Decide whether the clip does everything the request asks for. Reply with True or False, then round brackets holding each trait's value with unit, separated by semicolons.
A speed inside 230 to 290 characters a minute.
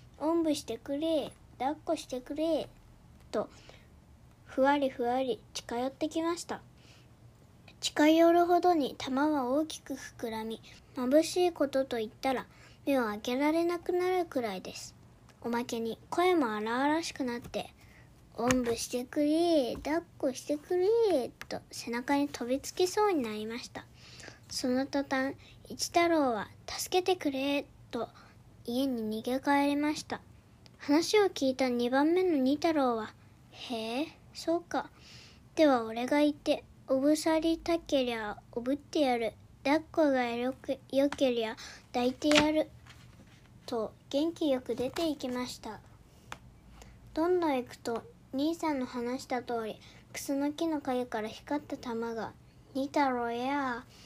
True (260 characters per minute)